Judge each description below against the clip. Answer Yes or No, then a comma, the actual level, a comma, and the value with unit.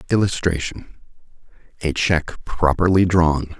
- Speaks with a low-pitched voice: Yes, very low, 85 Hz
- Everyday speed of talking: No, slow, 85 wpm